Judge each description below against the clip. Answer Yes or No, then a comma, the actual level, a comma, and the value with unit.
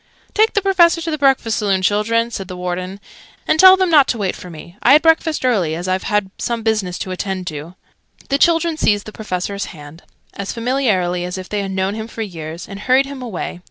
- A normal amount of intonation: No, wide, 6.8 semitones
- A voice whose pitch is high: Yes, high, 205 Hz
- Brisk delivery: Yes, fast, 220 wpm